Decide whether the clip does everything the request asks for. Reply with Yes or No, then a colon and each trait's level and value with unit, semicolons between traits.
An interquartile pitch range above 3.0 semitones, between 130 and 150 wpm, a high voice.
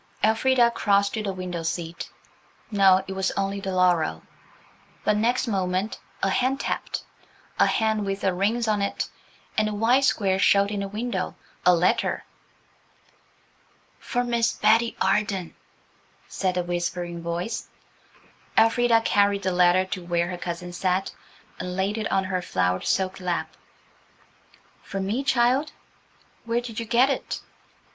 Yes: average, 3.6 semitones; average, 140 wpm; high, 195 Hz